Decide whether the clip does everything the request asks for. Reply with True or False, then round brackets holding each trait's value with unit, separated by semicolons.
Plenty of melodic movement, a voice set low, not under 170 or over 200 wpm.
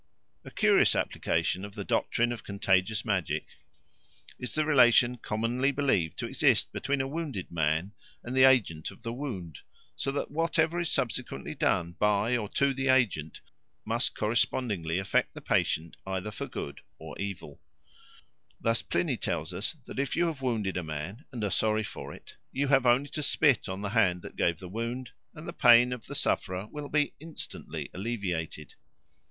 True (6.2 semitones; 115 Hz; 175 wpm)